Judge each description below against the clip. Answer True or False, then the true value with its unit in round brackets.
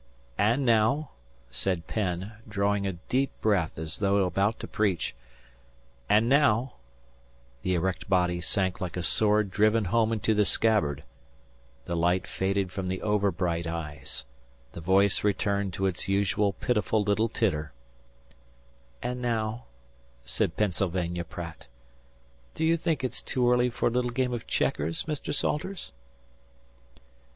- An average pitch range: True (4.1 semitones)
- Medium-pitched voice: False (100 Hz)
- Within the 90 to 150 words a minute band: True (135 wpm)